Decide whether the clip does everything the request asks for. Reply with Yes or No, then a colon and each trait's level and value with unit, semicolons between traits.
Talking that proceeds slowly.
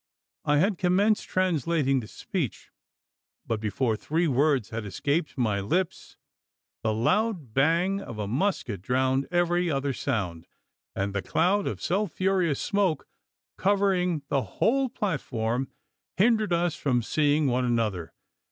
Yes: slow, 130 wpm